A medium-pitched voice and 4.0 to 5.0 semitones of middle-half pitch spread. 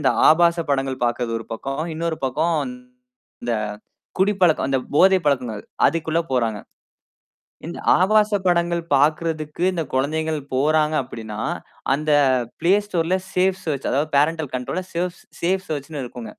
Yes: medium, 155 Hz; average, 4.3 semitones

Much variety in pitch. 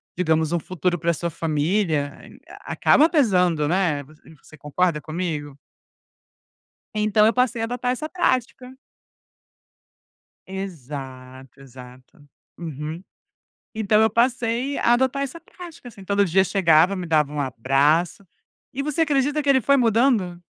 Yes: wide, 8.0 semitones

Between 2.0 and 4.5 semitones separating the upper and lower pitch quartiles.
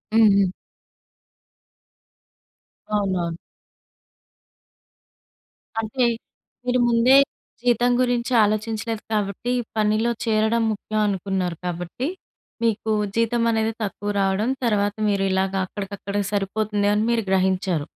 Yes: average, 2.8 semitones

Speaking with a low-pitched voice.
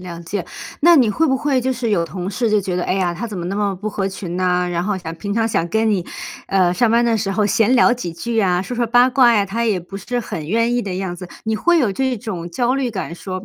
No: high, 205 Hz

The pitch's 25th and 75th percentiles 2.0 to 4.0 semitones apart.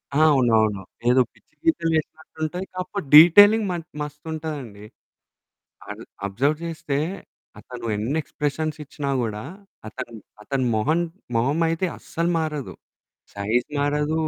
No: average, 4.6 semitones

